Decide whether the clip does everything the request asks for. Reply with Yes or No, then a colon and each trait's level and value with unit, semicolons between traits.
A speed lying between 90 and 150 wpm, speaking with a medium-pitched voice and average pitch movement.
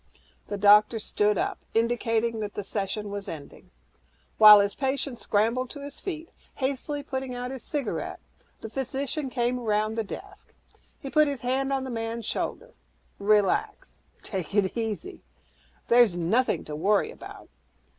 No: average, 145 wpm; high, 230 Hz; average, 4.3 semitones